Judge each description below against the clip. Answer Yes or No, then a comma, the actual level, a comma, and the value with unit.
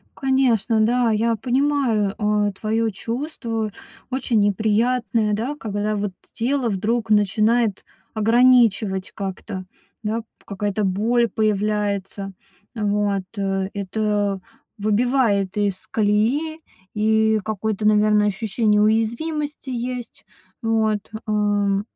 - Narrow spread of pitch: Yes, narrow, 2.3 semitones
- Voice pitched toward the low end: No, high, 215 Hz